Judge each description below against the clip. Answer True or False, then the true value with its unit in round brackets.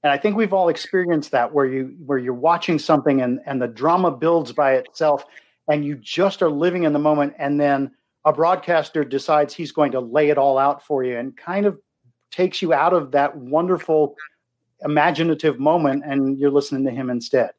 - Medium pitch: True (150 Hz)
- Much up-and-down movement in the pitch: False (3.3 semitones)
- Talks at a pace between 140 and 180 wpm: False (200 wpm)